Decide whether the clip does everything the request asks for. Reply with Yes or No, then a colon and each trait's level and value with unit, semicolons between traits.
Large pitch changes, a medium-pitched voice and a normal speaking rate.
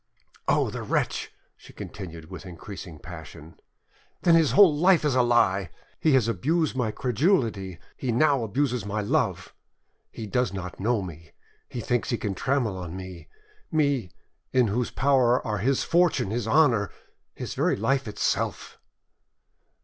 No: wide, 6.2 semitones; low, 115 Hz; average, 150 wpm